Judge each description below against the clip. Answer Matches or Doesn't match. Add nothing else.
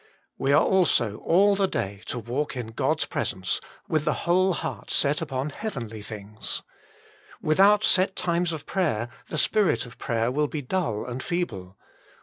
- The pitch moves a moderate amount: Doesn't match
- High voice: Doesn't match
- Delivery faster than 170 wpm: Doesn't match